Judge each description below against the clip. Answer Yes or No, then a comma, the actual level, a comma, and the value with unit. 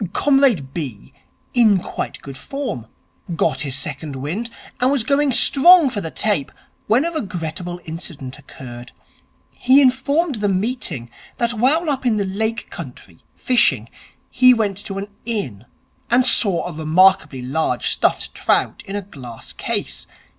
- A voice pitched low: No, high, 195 Hz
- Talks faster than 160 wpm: No, average, 145 wpm